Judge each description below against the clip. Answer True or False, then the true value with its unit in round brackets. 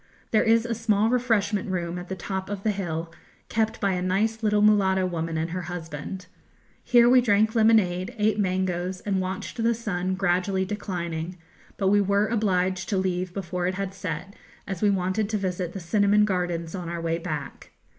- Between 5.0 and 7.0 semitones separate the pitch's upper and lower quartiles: False (2.8 semitones)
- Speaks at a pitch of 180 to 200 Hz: True (190 Hz)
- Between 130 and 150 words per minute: False (185 wpm)